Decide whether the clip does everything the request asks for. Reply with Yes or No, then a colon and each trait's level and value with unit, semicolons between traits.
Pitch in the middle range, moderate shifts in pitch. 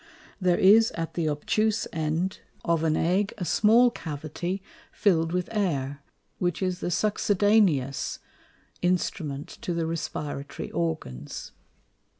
Yes: medium, 175 Hz; average, 4.0 semitones